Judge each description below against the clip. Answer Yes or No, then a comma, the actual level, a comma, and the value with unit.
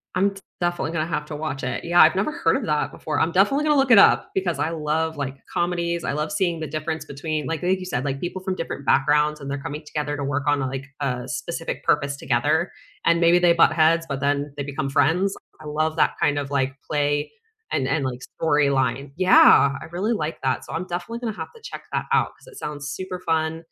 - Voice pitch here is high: No, medium, 155 Hz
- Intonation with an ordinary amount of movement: Yes, average, 3.4 semitones